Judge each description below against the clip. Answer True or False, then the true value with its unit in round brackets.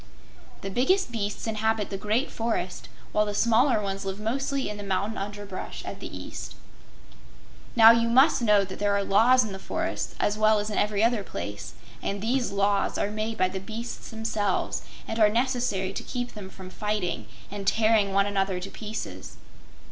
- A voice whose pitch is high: True (210 Hz)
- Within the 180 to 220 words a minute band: True (185 wpm)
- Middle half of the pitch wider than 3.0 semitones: False (2.5 semitones)